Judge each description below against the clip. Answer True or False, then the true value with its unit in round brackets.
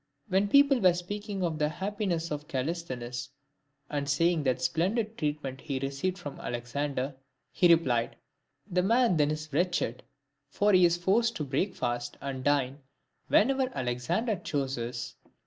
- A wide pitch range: True (5.8 semitones)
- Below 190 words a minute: True (145 wpm)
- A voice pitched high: False (155 Hz)